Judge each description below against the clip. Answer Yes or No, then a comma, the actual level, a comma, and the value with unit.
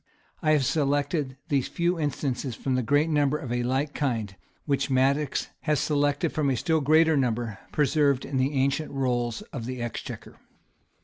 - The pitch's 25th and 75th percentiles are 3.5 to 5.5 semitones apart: No, average, 2.8 semitones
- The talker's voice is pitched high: No, medium, 140 Hz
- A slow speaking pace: No, average, 175 wpm